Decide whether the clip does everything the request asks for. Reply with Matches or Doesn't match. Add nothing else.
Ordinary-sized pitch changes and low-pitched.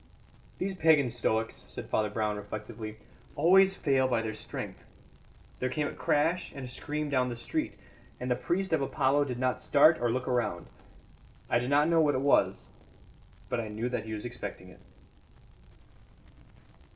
Matches